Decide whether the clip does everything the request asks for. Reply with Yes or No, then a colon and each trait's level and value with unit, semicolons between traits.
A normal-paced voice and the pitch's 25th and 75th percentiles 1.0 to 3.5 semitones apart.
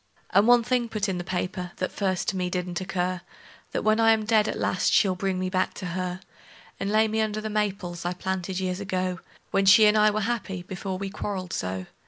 No: fast, 230 wpm; average, 2.7 semitones